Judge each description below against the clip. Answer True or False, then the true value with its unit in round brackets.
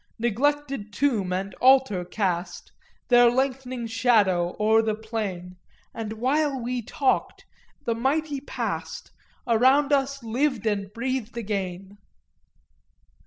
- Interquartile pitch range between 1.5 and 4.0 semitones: False (4.4 semitones)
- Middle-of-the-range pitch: False (230 Hz)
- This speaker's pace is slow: True (110 wpm)